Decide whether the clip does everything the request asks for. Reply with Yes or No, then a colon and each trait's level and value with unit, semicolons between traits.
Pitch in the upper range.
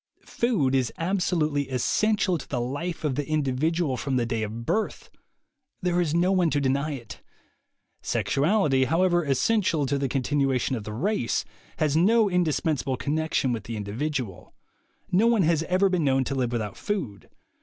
No: medium, 145 Hz